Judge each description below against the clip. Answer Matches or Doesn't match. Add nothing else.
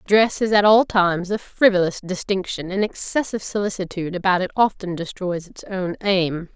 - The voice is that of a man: Doesn't match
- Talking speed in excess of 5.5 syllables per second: Doesn't match